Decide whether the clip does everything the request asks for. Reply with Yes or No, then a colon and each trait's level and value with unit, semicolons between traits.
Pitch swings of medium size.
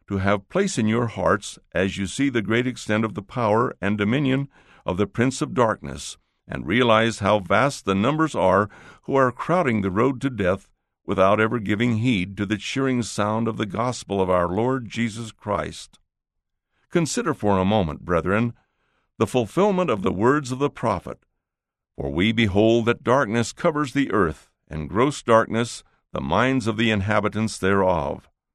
Yes: average, 4.1 semitones